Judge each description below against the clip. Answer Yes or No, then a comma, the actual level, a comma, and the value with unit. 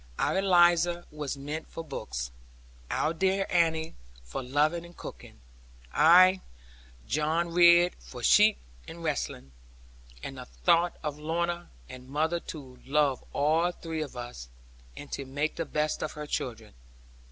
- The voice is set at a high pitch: No, medium, 155 Hz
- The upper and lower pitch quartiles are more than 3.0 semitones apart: Yes, average, 3.7 semitones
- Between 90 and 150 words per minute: Yes, average, 140 wpm